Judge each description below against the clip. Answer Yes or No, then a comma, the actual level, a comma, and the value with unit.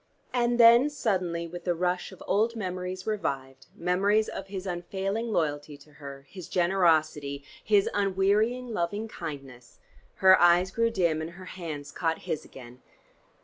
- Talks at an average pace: Yes, average, 145 wpm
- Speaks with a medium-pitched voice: Yes, medium, 180 Hz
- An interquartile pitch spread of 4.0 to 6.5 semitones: Yes, average, 4.5 semitones